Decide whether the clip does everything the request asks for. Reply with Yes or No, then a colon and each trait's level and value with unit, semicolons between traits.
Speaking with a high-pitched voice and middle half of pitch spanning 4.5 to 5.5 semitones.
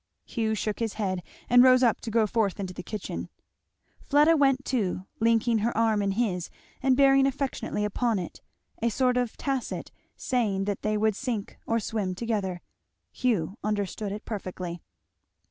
No: high, 220 Hz; average, 3.7 semitones